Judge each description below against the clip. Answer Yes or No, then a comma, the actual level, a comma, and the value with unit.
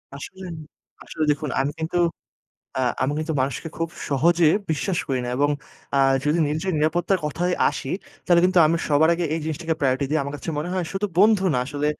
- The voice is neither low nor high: Yes, medium, 160 Hz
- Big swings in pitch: No, average, 3.3 semitones